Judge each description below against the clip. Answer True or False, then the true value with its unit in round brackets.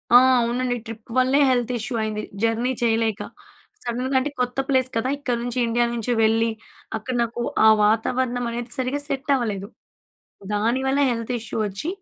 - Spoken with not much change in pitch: True (2.2 semitones)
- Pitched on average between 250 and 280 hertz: False (240 Hz)